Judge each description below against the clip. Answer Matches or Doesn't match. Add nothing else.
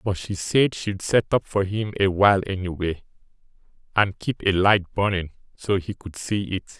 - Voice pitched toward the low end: Matches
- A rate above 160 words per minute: Matches